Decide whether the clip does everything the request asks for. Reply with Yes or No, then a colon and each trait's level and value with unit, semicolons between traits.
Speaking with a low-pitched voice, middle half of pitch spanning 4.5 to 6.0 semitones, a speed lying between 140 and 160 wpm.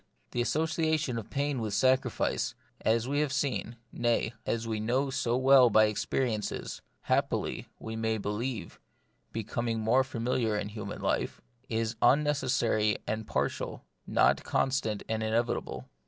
No: low, 115 Hz; average, 3.2 semitones; average, 145 wpm